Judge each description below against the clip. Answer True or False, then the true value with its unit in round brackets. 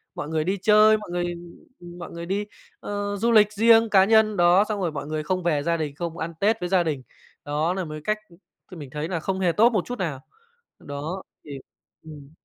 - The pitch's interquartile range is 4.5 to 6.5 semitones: True (4.8 semitones)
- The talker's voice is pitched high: False (175 Hz)